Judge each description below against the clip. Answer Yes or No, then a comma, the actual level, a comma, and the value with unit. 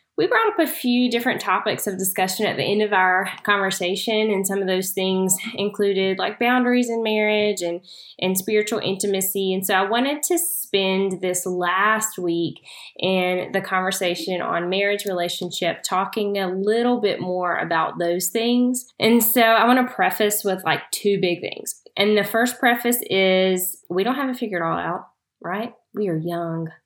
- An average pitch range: Yes, average, 3.4 semitones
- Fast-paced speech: No, average, 175 wpm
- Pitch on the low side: No, high, 195 Hz